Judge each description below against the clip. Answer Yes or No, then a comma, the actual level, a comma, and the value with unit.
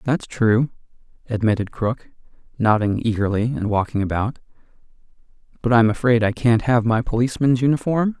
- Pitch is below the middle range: Yes, low, 115 Hz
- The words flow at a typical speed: No, slow, 130 wpm